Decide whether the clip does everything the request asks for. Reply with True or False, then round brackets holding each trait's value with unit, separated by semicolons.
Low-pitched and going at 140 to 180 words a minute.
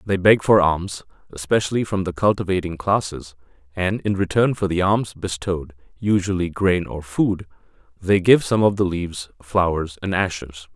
True (90 Hz; 160 wpm)